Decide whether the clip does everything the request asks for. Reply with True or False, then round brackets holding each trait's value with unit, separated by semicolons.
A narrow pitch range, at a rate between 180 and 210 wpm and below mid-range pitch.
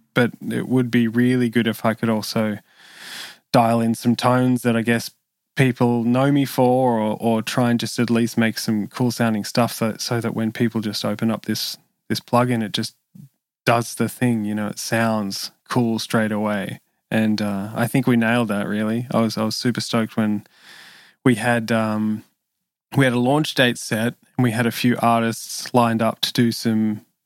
True (1.8 semitones; 200 wpm; 115 Hz)